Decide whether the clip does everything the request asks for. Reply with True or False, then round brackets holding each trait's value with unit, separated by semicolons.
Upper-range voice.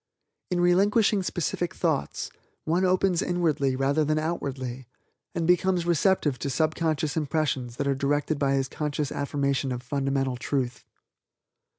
False (150 Hz)